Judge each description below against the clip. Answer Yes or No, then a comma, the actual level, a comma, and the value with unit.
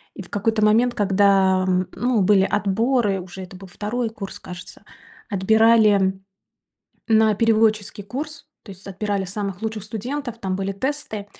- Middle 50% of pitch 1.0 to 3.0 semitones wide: Yes, narrow, 2.6 semitones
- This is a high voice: Yes, high, 205 Hz